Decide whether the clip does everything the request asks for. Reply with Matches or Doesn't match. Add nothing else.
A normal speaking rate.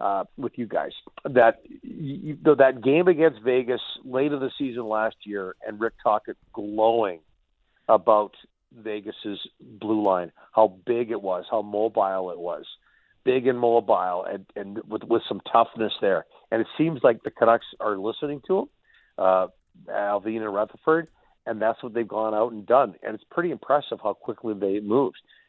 Matches